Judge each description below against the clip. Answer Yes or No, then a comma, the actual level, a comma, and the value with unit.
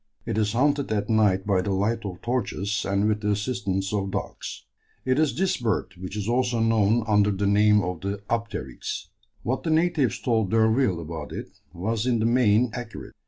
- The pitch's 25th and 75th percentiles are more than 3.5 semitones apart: No, average, 3.2 semitones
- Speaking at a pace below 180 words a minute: No, average, 190 wpm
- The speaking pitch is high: No, low, 105 Hz